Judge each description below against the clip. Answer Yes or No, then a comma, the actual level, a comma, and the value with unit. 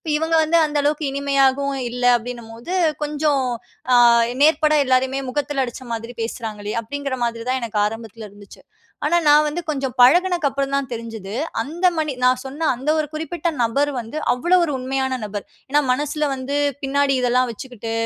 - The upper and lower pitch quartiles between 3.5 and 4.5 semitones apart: Yes, average, 3.9 semitones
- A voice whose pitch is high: Yes, very high, 270 Hz